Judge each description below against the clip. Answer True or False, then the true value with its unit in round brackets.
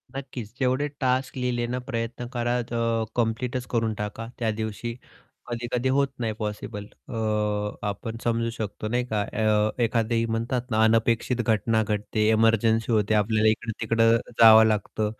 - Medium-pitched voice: False (115 Hz)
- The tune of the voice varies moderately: False (1.7 semitones)